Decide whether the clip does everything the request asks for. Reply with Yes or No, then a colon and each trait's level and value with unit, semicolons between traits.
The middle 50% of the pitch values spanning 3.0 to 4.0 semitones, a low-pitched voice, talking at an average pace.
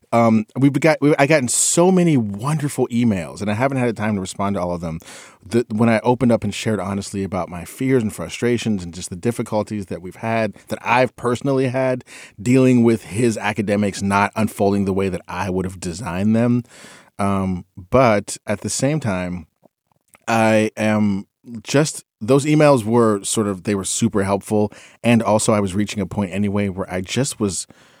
Yes: average, 3.5 semitones; low, 110 Hz; average, 195 wpm